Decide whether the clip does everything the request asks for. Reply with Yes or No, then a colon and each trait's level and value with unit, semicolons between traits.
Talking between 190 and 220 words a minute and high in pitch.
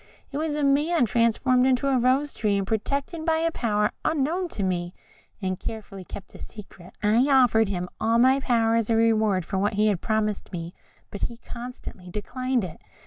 Yes: average, 195 wpm; high, 230 Hz